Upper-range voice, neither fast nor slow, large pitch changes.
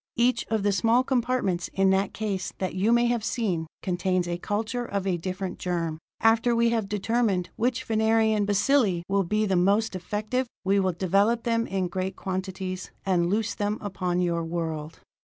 No: high, 200 Hz; average, 175 wpm; average, 3.6 semitones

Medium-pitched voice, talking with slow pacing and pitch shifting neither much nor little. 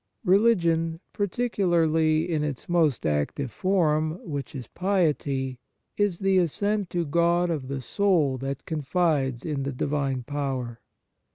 Yes: medium, 155 Hz; slow, 125 wpm; average, 4.5 semitones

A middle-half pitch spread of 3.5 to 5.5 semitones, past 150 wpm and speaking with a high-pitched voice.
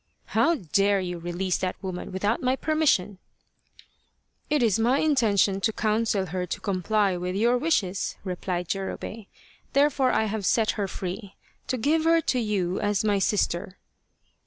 Yes: average, 4.1 semitones; average, 170 wpm; high, 205 Hz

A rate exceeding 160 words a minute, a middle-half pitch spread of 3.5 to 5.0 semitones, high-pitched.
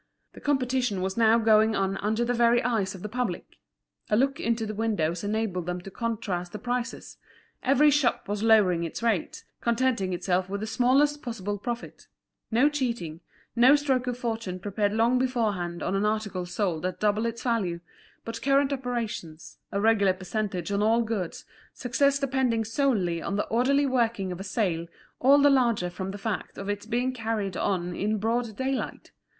Yes: average, 180 wpm; average, 4.1 semitones; high, 220 Hz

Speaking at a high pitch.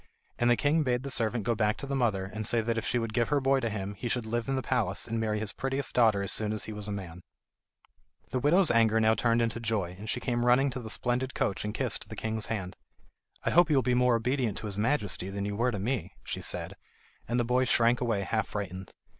No: low, 115 Hz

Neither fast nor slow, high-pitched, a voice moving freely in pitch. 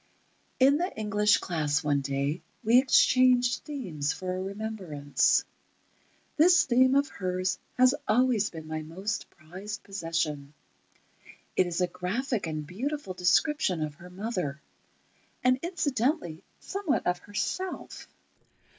No: slow, 120 wpm; high, 195 Hz; wide, 7.6 semitones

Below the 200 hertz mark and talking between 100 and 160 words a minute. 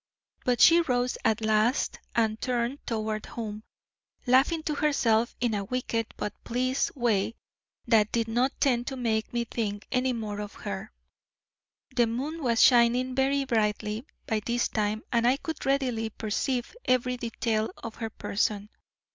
No: high, 235 Hz; average, 155 wpm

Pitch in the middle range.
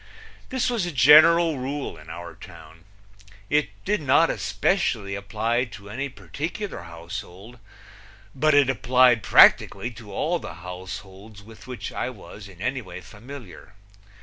No: low, 115 Hz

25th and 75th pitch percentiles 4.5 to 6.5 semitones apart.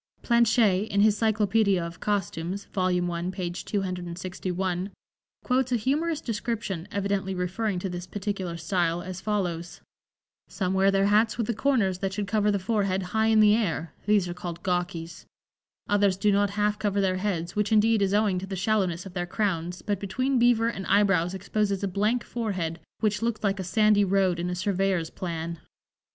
No: average, 2.8 semitones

